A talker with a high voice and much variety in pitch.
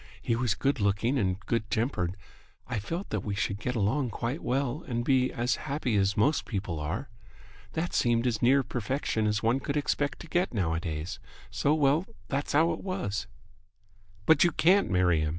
No: low, 120 Hz; wide, 5.8 semitones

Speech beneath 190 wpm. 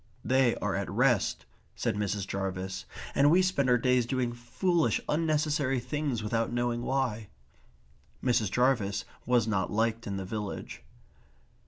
Yes: average, 140 wpm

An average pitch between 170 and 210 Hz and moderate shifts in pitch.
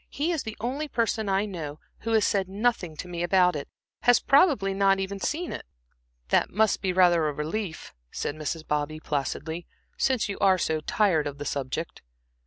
No: high, 190 Hz; wide, 5.7 semitones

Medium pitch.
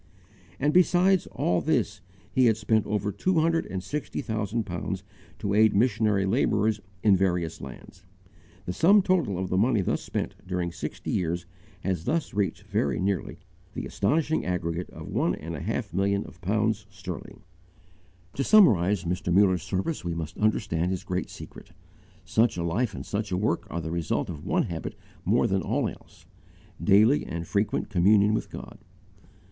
No: low, 100 Hz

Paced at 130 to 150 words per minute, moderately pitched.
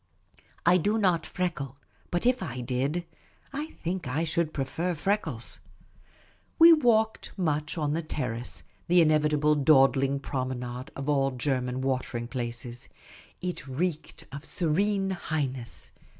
Yes: slow, 135 wpm; medium, 150 Hz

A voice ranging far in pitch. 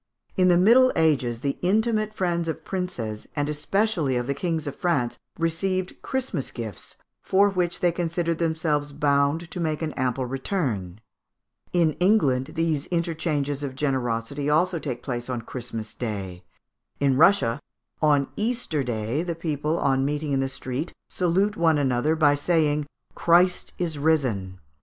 No: average, 4.7 semitones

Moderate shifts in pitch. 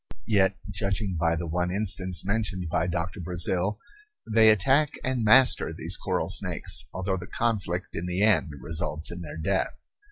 Yes: average, 3.4 semitones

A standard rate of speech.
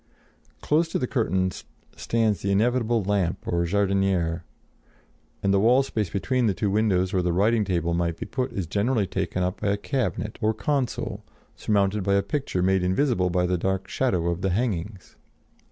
Yes: average, 180 wpm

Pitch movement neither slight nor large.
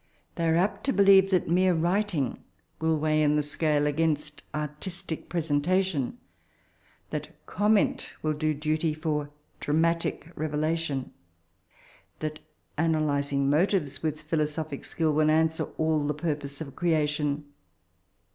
No: narrow, 2.0 semitones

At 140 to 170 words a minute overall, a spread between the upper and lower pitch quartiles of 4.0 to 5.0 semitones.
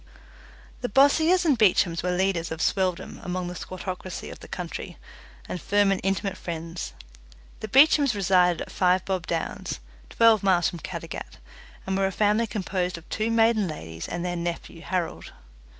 No: average, 165 wpm; average, 3.3 semitones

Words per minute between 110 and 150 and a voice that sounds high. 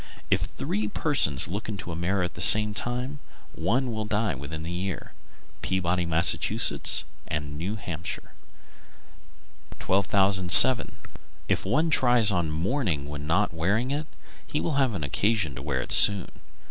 No: average, 145 wpm; very low, 95 Hz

